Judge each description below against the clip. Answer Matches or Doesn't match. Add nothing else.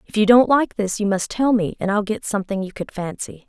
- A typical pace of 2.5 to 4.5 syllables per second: Doesn't match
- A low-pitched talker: Doesn't match